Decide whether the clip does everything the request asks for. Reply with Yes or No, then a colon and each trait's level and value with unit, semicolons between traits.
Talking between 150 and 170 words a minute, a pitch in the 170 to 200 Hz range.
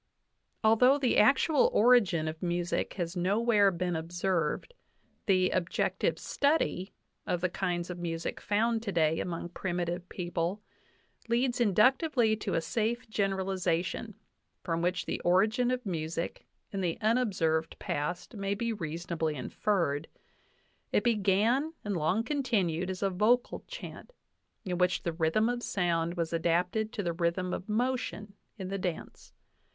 No: average, 140 wpm; medium, 185 Hz